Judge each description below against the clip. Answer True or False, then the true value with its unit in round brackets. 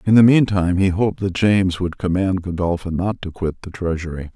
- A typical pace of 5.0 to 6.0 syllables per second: True (5.7 syllables/s)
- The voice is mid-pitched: False (95 Hz)